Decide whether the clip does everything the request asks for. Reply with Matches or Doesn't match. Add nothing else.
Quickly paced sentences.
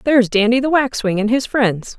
Matches